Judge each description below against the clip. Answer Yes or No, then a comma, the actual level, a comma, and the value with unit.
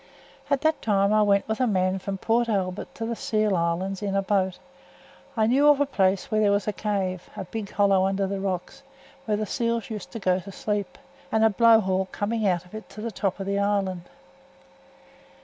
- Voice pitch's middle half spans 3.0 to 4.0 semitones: No, narrow, 2.4 semitones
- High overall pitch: Yes, high, 200 Hz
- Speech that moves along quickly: Yes, fast, 220 wpm